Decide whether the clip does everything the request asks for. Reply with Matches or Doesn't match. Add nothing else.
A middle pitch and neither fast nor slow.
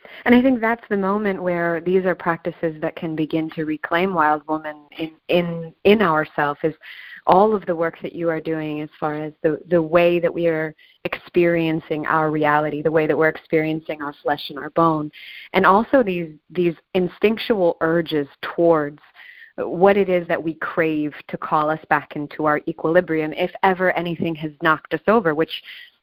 Matches